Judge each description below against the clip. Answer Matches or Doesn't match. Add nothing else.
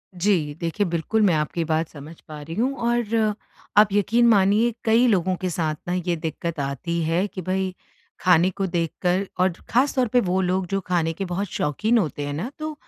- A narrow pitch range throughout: Doesn't match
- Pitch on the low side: Doesn't match